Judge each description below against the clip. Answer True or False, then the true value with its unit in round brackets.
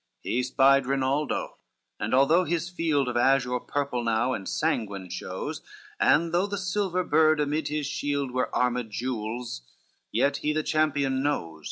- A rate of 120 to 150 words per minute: False (160 wpm)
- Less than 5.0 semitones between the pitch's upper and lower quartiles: True (3.9 semitones)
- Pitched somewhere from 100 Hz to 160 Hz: True (140 Hz)